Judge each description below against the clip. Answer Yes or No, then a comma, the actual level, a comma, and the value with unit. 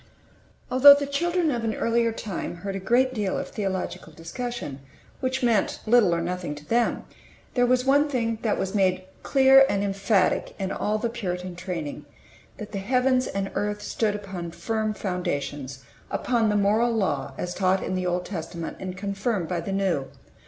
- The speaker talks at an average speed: Yes, average, 175 wpm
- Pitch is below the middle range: No, high, 200 Hz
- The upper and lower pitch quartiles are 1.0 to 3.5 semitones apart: No, average, 4.7 semitones